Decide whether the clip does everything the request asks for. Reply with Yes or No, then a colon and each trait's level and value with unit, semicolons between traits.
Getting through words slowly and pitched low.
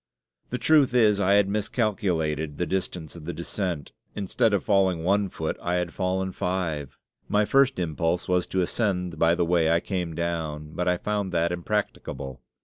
No: average, 175 wpm; very low, 90 Hz